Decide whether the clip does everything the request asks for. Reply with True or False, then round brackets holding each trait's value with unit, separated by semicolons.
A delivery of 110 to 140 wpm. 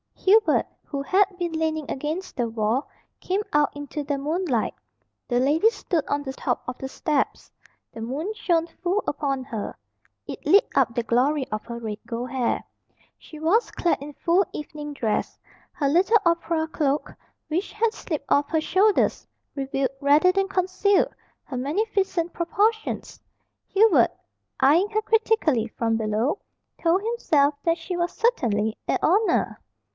False (150 wpm)